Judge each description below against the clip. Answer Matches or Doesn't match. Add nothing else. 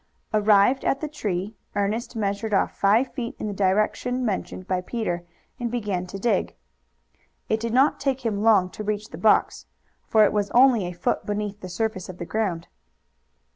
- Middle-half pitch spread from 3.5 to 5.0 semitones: Doesn't match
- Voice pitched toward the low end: Doesn't match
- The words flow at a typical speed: Matches